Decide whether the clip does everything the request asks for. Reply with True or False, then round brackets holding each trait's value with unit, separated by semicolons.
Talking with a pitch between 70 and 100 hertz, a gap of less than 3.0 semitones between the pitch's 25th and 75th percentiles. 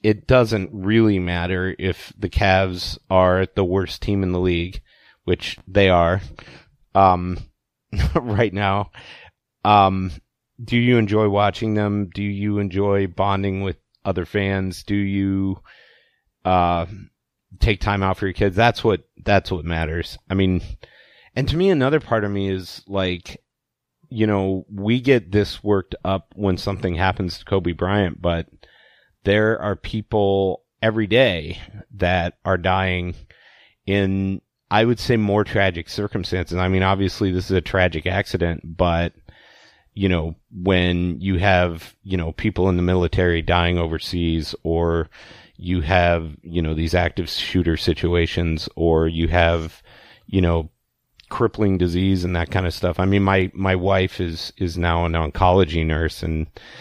True (95 Hz; 2.5 semitones)